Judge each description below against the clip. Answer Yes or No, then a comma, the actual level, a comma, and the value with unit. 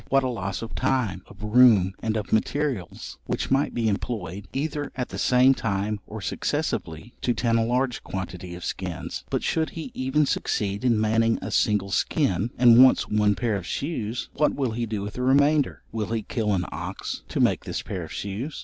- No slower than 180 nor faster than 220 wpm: Yes, average, 200 wpm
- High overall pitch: No, low, 115 Hz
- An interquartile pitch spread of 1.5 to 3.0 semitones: No, average, 4.2 semitones